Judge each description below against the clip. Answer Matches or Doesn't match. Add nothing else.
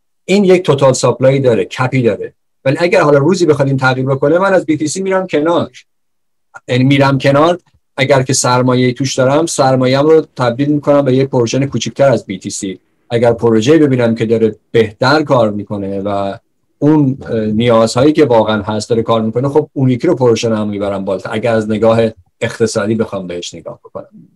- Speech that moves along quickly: Matches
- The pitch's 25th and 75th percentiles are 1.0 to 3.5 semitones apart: Doesn't match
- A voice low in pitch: Matches